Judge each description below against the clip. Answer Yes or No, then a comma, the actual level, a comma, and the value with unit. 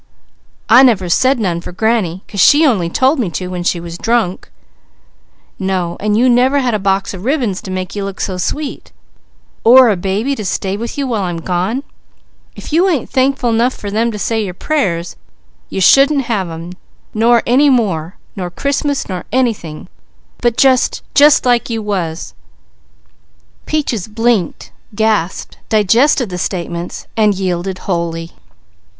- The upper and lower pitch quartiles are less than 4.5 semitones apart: No, wide, 5.4 semitones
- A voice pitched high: Yes, high, 210 Hz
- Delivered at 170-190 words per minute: No, average, 160 wpm